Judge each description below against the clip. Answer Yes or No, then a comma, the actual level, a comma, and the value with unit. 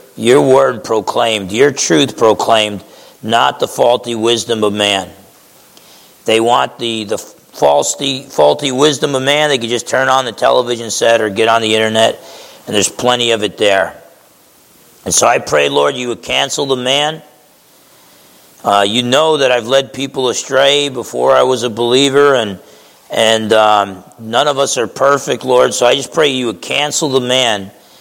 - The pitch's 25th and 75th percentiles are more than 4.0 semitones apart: No, average, 3.6 semitones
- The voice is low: Yes, low, 120 Hz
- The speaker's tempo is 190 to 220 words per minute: No, average, 175 wpm